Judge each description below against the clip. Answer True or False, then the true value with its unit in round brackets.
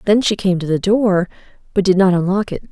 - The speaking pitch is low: False (190 Hz)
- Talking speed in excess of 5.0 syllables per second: True (5.8 syllables/s)